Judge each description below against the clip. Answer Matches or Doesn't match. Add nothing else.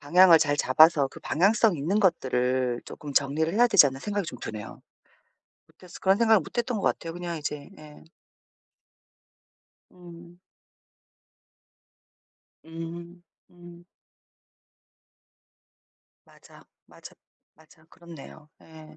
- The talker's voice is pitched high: Doesn't match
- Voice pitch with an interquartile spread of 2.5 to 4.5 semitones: Matches